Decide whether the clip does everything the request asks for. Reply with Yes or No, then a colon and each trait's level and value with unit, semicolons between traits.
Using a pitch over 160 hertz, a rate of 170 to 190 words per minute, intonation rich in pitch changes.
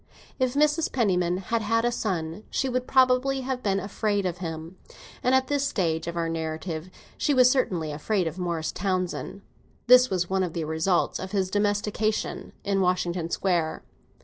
Yes: high, 190 Hz; average, 175 wpm; wide, 6.0 semitones